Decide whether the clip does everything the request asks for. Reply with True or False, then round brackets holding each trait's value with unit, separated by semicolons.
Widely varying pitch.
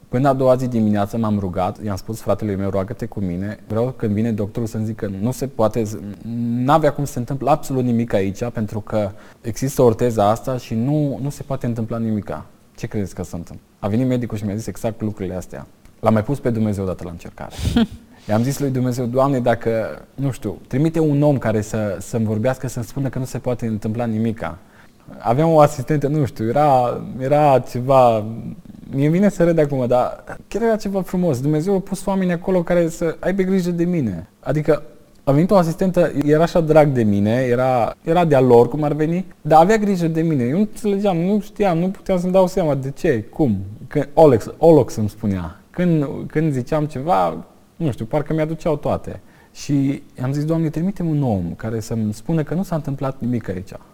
True (6.0 semitones)